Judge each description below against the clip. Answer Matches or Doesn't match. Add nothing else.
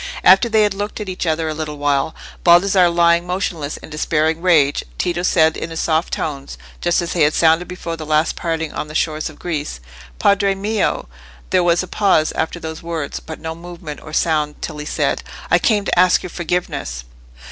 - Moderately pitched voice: Matches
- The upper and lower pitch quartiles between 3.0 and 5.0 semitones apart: Doesn't match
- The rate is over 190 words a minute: Matches